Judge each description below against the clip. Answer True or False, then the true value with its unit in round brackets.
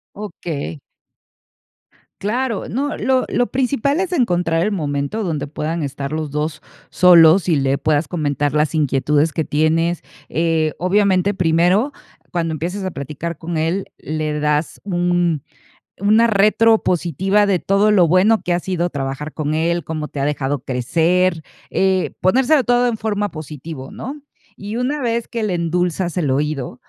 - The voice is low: False (170 Hz)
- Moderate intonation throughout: True (5.0 semitones)